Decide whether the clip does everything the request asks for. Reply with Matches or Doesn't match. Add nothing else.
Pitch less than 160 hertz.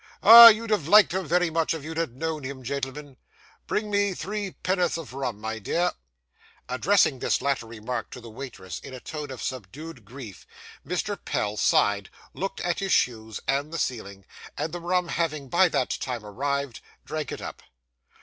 Matches